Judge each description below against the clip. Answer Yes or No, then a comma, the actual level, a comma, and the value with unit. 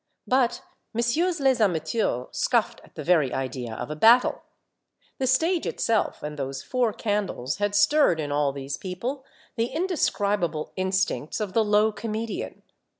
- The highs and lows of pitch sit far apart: Yes, wide, 7.8 semitones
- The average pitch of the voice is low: No, high, 205 Hz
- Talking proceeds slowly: No, average, 150 wpm